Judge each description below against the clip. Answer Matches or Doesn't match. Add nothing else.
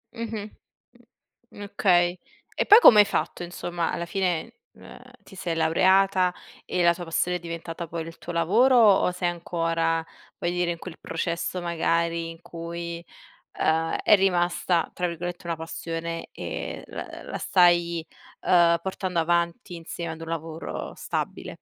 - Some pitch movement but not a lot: Doesn't match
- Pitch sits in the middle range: Matches